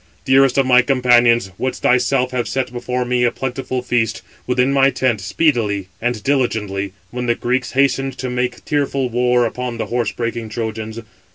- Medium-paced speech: Yes, average, 170 wpm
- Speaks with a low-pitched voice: Yes, low, 125 Hz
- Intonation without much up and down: Yes, narrow, 1.8 semitones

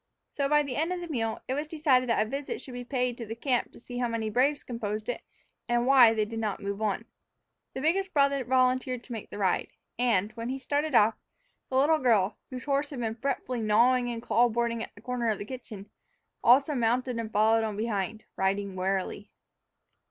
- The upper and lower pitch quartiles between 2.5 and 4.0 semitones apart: Yes, average, 3.2 semitones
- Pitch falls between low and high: No, high, 240 Hz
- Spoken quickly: Yes, fast, 210 wpm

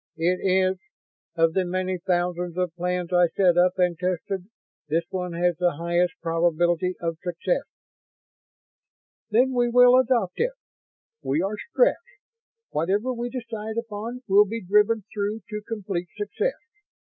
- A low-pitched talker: No, medium, 185 Hz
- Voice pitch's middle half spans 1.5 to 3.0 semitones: No, average, 3.8 semitones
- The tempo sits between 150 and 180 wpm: No, average, 140 wpm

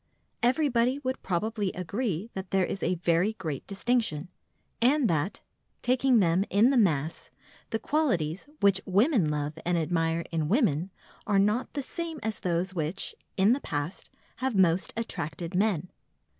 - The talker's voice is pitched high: Yes, high, 195 Hz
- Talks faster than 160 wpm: No, average, 150 wpm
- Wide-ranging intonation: Yes, wide, 5.9 semitones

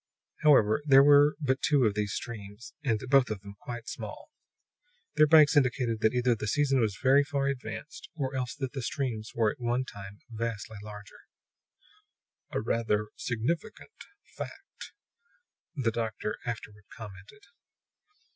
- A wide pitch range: No, average, 4.3 semitones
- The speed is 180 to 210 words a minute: No, average, 145 wpm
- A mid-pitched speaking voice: No, low, 120 Hz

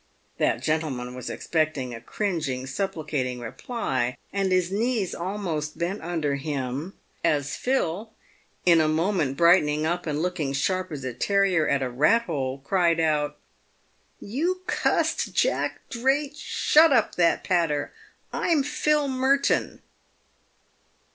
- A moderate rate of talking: No, slow, 130 wpm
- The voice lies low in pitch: No, medium, 165 Hz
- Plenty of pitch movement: Yes, wide, 5.8 semitones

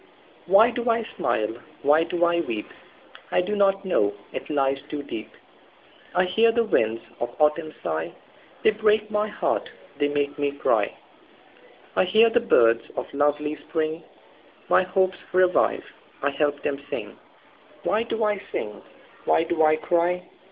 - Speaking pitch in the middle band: Yes, medium, 170 Hz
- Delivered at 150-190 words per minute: No, slow, 135 wpm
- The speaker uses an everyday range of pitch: No, wide, 6.4 semitones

